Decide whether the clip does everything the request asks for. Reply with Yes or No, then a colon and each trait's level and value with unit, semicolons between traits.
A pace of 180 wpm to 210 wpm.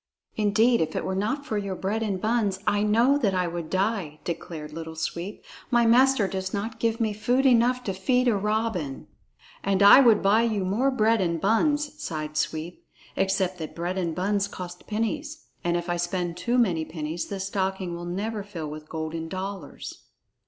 Yes: average, 190 wpm